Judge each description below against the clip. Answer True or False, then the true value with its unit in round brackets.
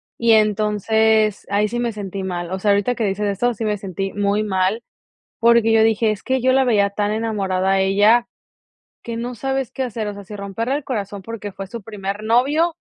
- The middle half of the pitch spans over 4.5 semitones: False (2.7 semitones)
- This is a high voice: True (215 Hz)